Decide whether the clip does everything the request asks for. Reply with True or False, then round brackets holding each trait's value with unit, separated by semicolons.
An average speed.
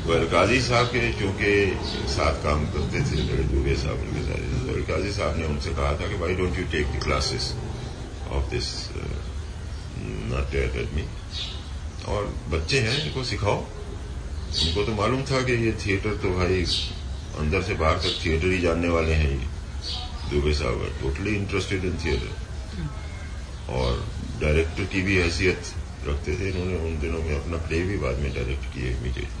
True (155 wpm)